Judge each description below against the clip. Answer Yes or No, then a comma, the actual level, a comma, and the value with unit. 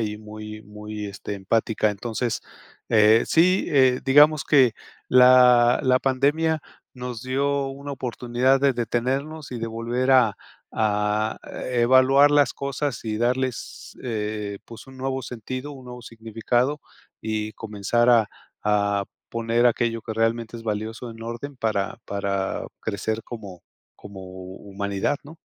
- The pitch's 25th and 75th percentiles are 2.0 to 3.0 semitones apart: No, average, 3.5 semitones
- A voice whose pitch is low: Yes, low, 115 Hz